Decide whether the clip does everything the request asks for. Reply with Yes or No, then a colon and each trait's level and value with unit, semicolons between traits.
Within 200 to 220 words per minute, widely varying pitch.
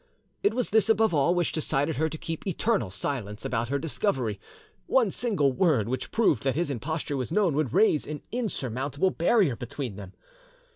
No: average, 180 wpm; wide, 6.7 semitones